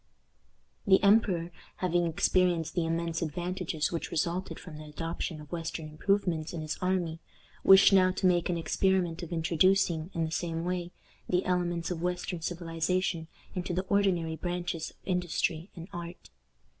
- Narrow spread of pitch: Yes, narrow, 1.9 semitones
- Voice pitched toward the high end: No, medium, 175 Hz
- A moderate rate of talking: Yes, average, 155 wpm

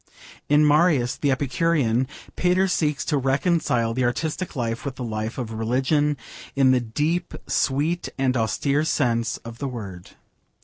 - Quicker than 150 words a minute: No, average, 145 wpm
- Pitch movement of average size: Yes, average, 4.2 semitones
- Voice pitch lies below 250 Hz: Yes, low, 135 Hz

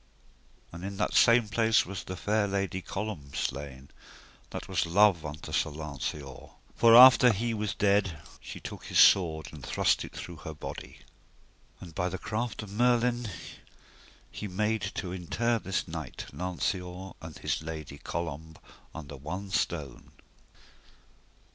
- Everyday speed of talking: Yes, average, 145 wpm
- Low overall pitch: Yes, very low, 95 Hz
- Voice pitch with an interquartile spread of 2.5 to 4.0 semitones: No, average, 5.1 semitones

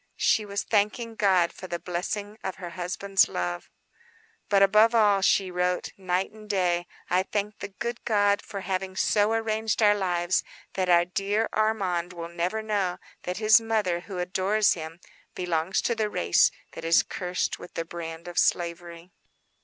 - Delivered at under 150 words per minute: No, average, 170 wpm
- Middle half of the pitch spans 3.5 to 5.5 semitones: No, average, 3.1 semitones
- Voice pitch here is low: No, high, 190 Hz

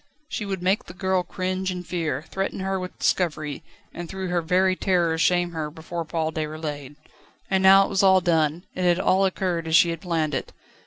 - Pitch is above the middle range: No, medium, 175 Hz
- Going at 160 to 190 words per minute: No, fast, 205 wpm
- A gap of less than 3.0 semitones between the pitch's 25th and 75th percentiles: Yes, narrow, 2.6 semitones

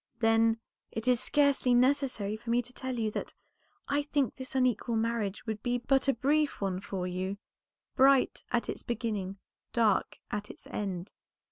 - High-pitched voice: Yes, high, 235 Hz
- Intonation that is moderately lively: Yes, average, 3.7 semitones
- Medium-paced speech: Yes, average, 165 wpm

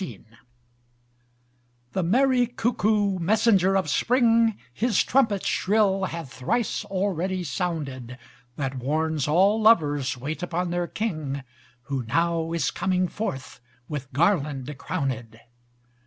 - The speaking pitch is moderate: Yes, medium, 175 Hz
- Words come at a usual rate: No, slow, 110 wpm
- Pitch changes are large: Yes, wide, 6.3 semitones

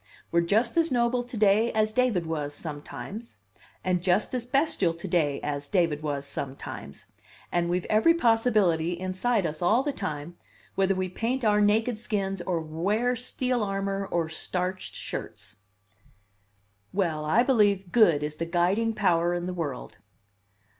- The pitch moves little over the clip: No, average, 5.2 semitones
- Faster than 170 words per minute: No, average, 155 wpm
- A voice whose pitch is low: No, high, 190 Hz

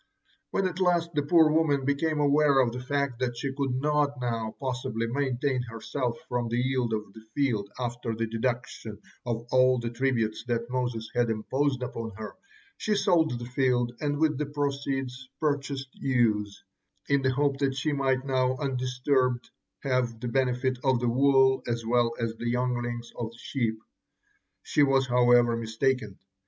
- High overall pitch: No, low, 130 Hz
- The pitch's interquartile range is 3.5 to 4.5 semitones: No, average, 2.8 semitones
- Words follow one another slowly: No, average, 170 wpm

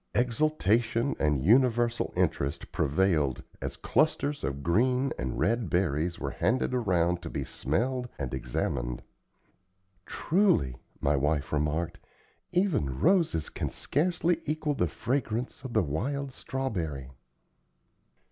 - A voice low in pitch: Yes, low, 105 Hz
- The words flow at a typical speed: No, slow, 115 wpm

